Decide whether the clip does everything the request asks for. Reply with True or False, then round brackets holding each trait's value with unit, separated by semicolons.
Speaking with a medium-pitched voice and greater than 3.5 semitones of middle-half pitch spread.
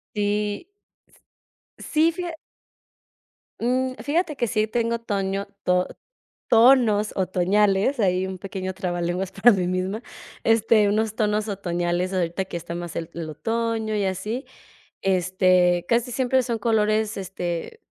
False (205 Hz; 3.9 semitones)